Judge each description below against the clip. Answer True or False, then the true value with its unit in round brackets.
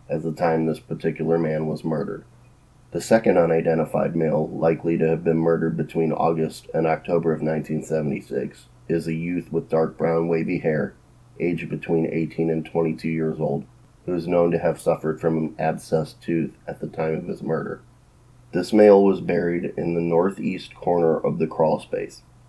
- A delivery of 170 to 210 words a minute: True (175 wpm)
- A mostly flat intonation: True (1.2 semitones)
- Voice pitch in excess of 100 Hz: False (80 Hz)